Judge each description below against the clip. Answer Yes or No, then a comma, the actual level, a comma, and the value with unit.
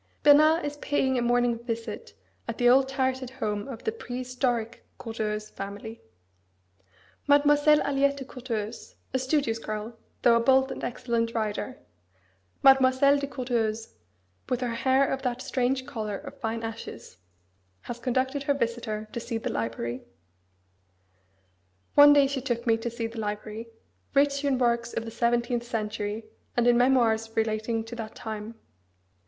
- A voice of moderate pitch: No, high, 240 Hz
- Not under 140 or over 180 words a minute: Yes, average, 150 wpm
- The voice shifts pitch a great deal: No, average, 2.9 semitones